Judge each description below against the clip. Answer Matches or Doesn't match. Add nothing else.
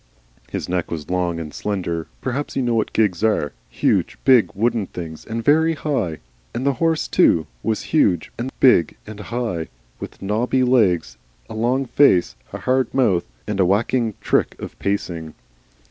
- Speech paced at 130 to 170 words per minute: Matches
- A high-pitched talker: Doesn't match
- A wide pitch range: Matches